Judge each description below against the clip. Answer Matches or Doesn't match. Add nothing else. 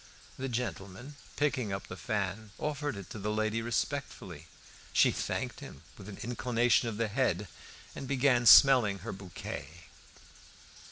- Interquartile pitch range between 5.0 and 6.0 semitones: Doesn't match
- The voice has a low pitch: Matches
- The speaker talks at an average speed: Matches